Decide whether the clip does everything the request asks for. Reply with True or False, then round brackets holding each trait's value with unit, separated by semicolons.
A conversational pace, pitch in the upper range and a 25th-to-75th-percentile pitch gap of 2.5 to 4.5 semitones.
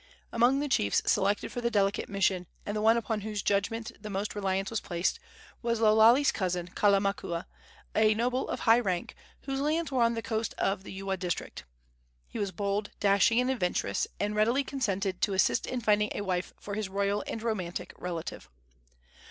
True (185 wpm; 205 Hz; 3.0 semitones)